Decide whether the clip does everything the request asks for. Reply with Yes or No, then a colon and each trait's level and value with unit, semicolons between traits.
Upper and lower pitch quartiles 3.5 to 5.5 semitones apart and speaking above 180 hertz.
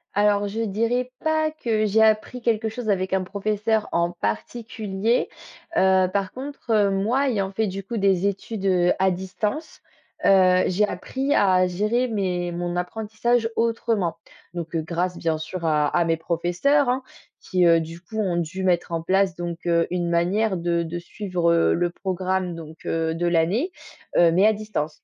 Yes: average, 3.9 semitones; high, 190 Hz